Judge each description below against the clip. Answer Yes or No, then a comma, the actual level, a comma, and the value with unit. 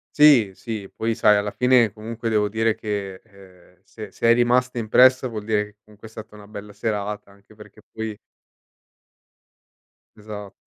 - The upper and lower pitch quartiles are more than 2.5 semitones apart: No, narrow, 1.8 semitones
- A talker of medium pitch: No, low, 105 Hz